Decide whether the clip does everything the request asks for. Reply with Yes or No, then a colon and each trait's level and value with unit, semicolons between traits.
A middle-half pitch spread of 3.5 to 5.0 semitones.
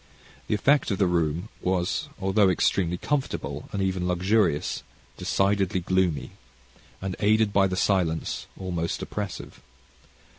No: narrow, 2.4 semitones